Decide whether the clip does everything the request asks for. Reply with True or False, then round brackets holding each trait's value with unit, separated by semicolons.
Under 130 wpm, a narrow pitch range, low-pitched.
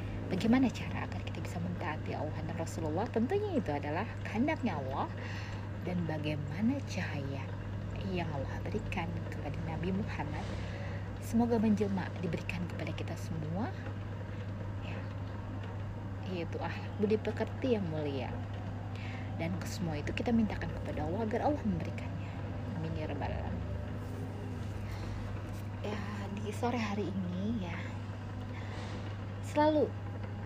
True (110 wpm; 1.2 semitones; 100 Hz)